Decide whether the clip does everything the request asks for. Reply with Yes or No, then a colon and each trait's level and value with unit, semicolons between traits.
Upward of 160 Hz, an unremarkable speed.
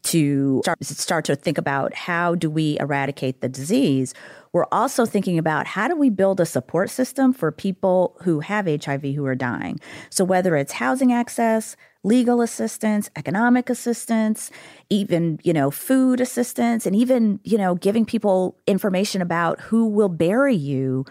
Yes: medium, 185 Hz; average, 160 wpm